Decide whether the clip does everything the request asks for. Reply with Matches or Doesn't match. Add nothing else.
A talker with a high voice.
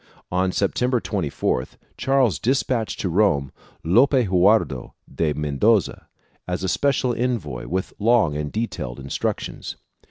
Doesn't match